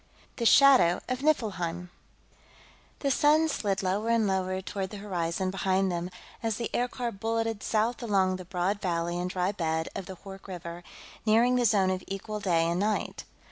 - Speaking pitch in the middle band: No, high, 195 Hz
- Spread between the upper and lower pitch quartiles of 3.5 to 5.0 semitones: Yes, average, 3.8 semitones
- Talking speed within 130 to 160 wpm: No, average, 175 wpm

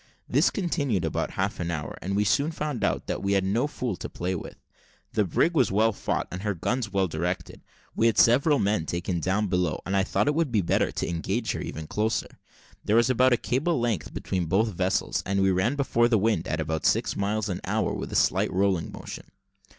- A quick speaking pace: Yes, fast, 220 wpm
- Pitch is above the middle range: No, low, 100 Hz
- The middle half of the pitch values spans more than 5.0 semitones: No, average, 4.7 semitones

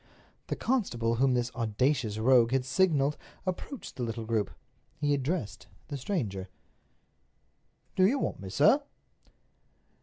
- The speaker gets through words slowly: Yes, slow, 125 wpm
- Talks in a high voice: No, low, 130 Hz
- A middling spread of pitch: Yes, average, 5.0 semitones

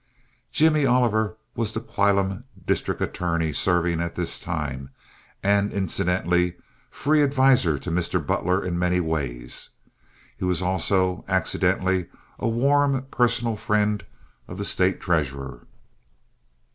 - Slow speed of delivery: Yes, slow, 120 wpm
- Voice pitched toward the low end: Yes, very low, 95 Hz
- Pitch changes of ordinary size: Yes, average, 4.4 semitones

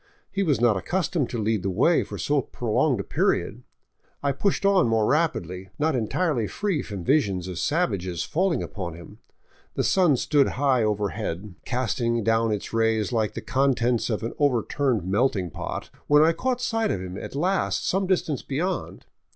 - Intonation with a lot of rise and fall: Yes, wide, 6.9 semitones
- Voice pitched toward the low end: Yes, low, 120 Hz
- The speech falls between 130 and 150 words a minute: No, average, 175 wpm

